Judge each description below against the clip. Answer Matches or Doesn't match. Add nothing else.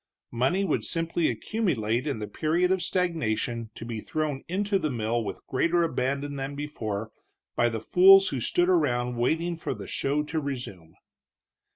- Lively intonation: Matches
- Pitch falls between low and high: Matches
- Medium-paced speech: Matches